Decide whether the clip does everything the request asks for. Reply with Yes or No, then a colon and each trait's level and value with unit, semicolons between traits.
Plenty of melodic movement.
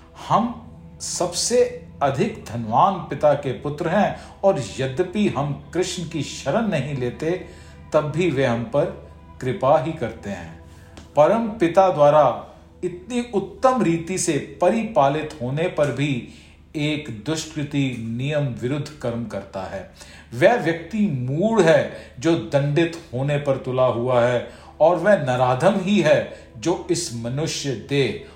Yes: wide, 6.0 semitones